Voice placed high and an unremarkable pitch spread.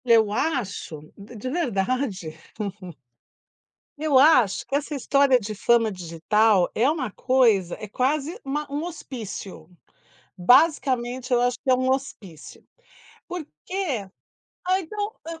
No: very high, 255 Hz; wide, 5.8 semitones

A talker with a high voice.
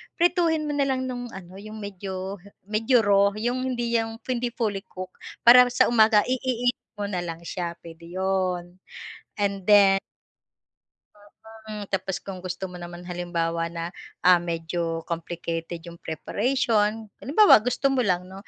Yes: high, 195 Hz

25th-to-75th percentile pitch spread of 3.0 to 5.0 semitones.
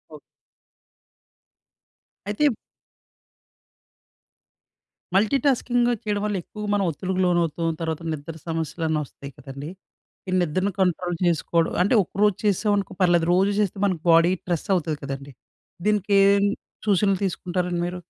Yes: average, 3.7 semitones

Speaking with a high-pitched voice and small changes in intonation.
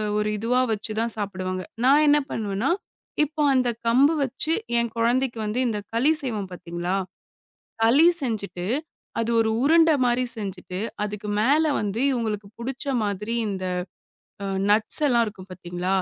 No: high, 225 Hz; average, 4.1 semitones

